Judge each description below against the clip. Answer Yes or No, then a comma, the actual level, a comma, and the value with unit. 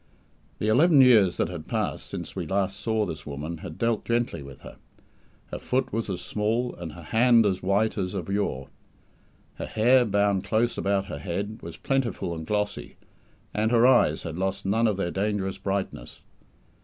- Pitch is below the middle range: Yes, low, 100 Hz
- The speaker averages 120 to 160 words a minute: No, average, 180 wpm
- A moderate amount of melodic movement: Yes, average, 3.6 semitones